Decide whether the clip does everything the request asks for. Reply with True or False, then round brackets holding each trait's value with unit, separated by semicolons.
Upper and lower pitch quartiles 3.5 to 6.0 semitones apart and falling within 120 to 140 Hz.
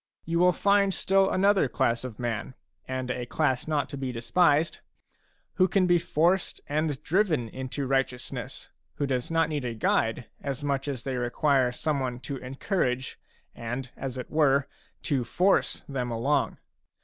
True (4.4 semitones; 135 Hz)